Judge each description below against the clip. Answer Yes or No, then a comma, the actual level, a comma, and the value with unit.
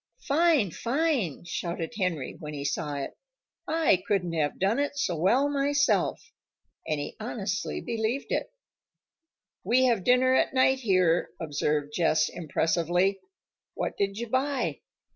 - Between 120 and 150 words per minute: Yes, slow, 135 wpm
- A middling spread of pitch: No, wide, 7.9 semitones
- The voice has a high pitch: Yes, high, 200 Hz